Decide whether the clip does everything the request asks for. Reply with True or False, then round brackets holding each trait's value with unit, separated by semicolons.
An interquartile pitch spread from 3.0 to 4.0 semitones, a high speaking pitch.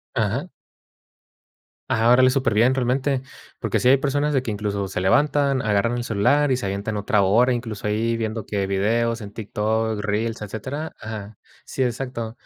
False (3.6 semitones; 115 Hz)